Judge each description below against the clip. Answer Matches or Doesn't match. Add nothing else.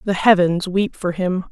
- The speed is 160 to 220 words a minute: Matches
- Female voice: Matches